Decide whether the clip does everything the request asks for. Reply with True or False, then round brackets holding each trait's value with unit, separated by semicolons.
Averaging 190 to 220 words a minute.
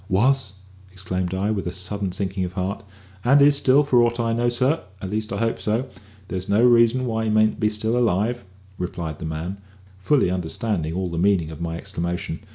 True (200 wpm)